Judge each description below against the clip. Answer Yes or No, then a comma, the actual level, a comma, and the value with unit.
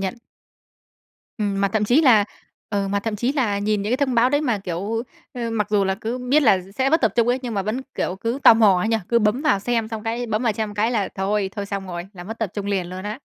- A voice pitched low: No, high, 215 Hz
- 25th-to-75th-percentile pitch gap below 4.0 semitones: Yes, average, 3.0 semitones